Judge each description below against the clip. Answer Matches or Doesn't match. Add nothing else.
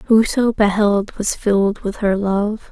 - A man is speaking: Doesn't match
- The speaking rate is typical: Matches